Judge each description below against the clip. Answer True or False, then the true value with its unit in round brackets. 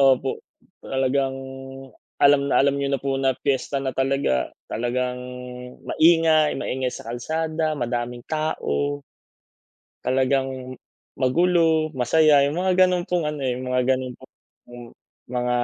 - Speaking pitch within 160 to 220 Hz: False (135 Hz)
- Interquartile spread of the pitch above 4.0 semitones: False (3.5 semitones)